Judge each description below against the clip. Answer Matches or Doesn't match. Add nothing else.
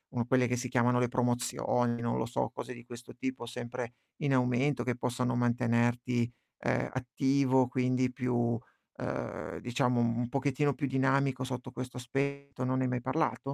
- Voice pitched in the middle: Doesn't match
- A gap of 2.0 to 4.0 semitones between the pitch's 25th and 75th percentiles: Doesn't match